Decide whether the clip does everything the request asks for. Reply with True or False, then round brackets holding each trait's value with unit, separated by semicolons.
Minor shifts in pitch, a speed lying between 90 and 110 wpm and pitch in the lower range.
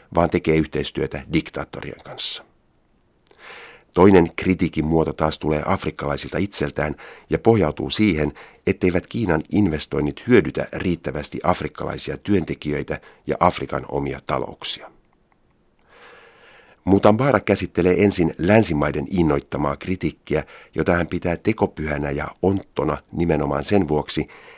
False (4.2 semitones; 100 wpm; 80 Hz)